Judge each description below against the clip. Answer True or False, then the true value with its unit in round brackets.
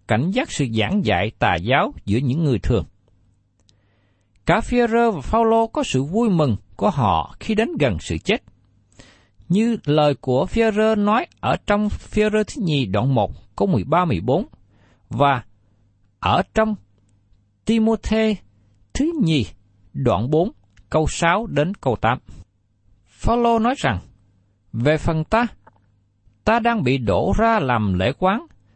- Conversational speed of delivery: False (140 wpm)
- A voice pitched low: True (125 Hz)